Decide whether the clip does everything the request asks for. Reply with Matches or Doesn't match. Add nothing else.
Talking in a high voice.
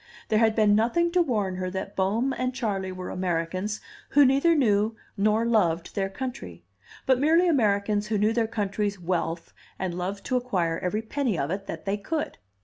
Matches